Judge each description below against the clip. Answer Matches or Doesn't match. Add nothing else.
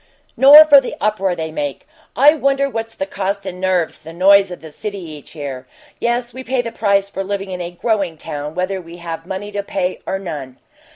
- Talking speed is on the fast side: Matches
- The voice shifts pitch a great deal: Doesn't match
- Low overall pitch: Doesn't match